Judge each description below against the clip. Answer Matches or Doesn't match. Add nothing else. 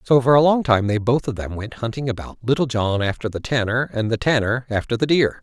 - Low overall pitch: Matches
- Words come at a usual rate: Doesn't match